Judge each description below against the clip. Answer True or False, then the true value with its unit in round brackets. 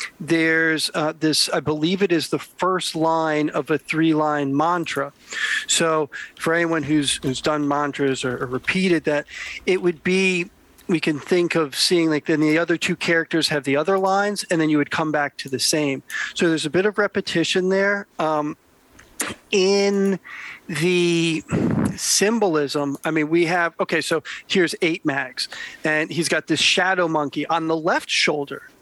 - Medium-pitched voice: True (165 Hz)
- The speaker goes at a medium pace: True (170 wpm)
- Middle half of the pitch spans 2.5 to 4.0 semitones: True (3.3 semitones)